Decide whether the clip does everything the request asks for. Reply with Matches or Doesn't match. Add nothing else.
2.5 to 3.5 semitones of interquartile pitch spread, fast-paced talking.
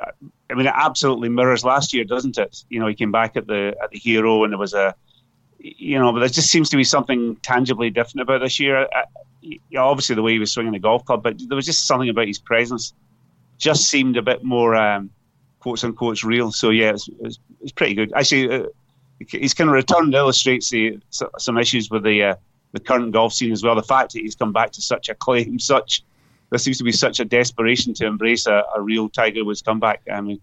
Matches